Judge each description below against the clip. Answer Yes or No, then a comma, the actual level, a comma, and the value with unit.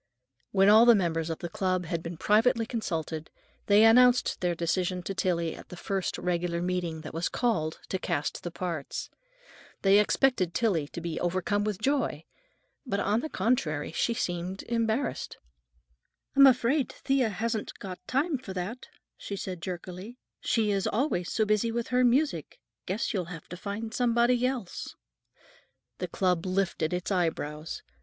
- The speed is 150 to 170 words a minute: Yes, average, 160 wpm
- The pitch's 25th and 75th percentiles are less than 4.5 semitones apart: No, average, 5.0 semitones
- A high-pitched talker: Yes, high, 195 Hz